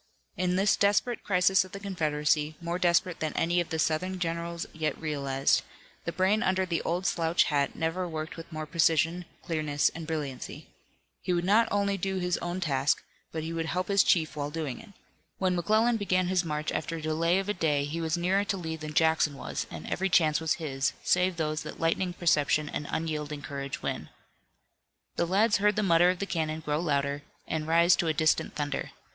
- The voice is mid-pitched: Yes, medium, 165 Hz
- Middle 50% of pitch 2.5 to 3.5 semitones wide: Yes, average, 3.0 semitones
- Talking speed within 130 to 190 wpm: No, average, 200 wpm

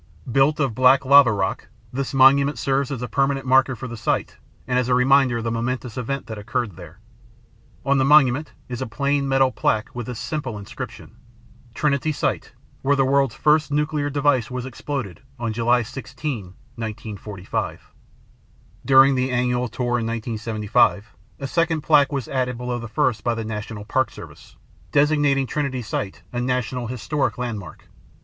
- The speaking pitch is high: No, low, 125 Hz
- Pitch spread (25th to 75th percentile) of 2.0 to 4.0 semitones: Yes, average, 3.0 semitones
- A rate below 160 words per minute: No, average, 165 wpm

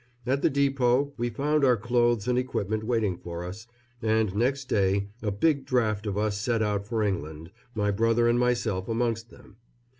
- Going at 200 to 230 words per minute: No, average, 180 wpm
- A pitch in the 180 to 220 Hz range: No, low, 115 Hz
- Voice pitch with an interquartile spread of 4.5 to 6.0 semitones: No, average, 3.3 semitones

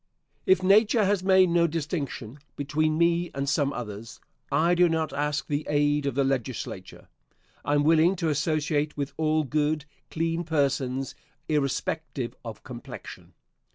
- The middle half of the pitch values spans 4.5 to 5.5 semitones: No, average, 3.0 semitones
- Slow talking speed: No, average, 145 wpm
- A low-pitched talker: No, medium, 150 Hz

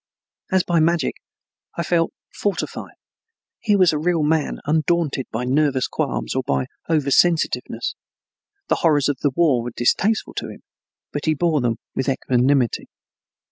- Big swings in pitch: No, average, 4.4 semitones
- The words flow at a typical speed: Yes, average, 150 wpm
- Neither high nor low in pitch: Yes, medium, 150 Hz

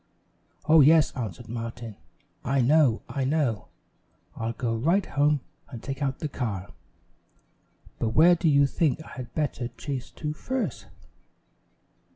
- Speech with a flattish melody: No, average, 4.5 semitones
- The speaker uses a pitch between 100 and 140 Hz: Yes, low, 135 Hz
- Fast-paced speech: No, average, 140 wpm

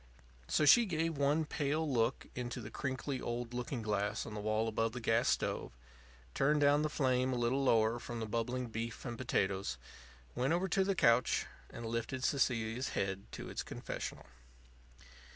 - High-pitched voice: No, low, 120 Hz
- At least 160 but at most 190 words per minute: Yes, average, 170 wpm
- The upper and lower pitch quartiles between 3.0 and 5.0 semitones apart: Yes, average, 3.7 semitones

